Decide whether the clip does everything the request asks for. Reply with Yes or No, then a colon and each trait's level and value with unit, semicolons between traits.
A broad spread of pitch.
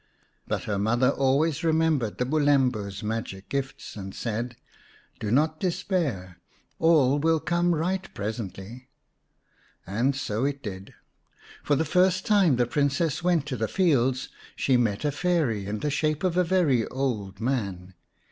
Yes: wide, 6.4 semitones